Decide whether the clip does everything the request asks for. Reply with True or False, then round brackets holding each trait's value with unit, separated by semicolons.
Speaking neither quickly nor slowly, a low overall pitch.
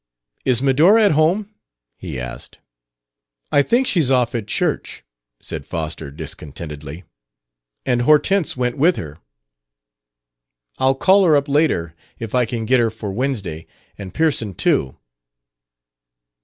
False (130 wpm; 125 Hz)